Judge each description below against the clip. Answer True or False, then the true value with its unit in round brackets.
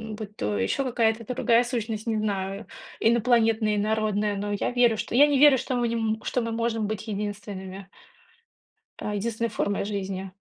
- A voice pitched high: True (220 Hz)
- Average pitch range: False (2.3 semitones)